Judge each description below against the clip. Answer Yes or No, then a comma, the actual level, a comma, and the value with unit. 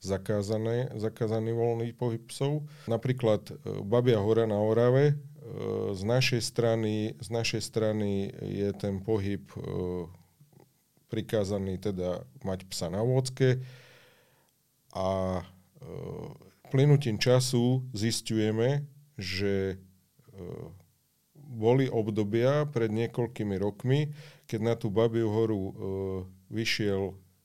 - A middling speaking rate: No, slow, 105 wpm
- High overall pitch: No, low, 115 Hz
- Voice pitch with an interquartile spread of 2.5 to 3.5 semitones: No, average, 3.9 semitones